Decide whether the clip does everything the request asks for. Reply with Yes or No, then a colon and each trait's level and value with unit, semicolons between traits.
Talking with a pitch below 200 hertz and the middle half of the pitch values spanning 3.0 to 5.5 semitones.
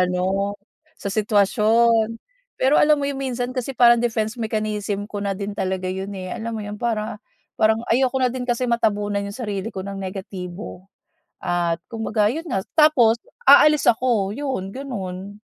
No: high, 215 Hz; average, 3.4 semitones